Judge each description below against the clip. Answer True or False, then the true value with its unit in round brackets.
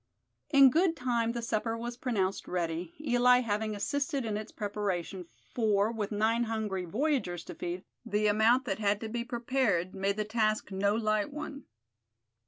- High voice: True (220 Hz)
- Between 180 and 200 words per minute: False (165 wpm)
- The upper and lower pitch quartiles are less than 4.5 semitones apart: True (3.2 semitones)